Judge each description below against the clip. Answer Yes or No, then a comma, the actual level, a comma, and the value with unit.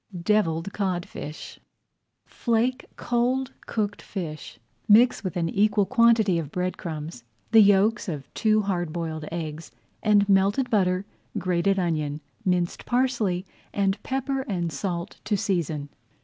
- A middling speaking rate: No, slow, 125 wpm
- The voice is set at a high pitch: Yes, high, 195 Hz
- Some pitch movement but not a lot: Yes, average, 4.1 semitones